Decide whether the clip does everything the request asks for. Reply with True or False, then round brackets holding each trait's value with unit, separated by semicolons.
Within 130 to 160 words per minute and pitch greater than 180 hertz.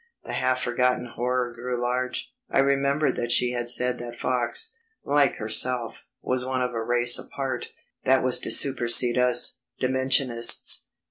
False (150 wpm; 125 Hz)